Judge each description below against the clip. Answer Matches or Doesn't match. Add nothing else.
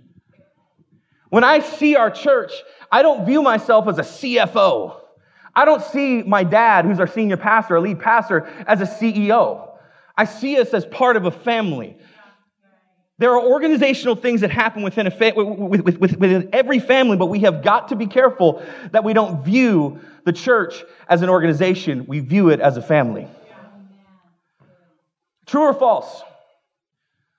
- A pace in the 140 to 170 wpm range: Matches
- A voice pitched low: Doesn't match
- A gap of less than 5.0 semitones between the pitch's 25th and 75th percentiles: Doesn't match